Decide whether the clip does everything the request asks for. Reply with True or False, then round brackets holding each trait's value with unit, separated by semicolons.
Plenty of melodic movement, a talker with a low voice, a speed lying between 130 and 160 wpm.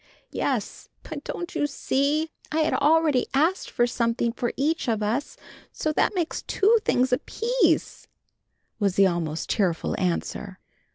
False (6.7 semitones; 275 Hz; 145 wpm)